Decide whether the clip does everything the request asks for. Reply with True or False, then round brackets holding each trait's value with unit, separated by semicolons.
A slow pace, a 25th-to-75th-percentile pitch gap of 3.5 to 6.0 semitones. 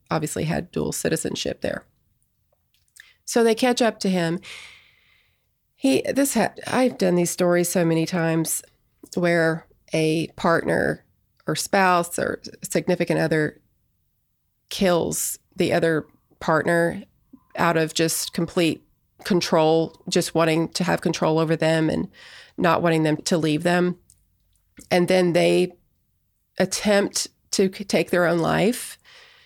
False (125 wpm; 2.5 semitones)